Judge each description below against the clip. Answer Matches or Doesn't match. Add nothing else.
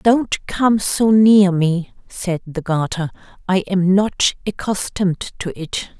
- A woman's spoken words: Matches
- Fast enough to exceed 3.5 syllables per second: Doesn't match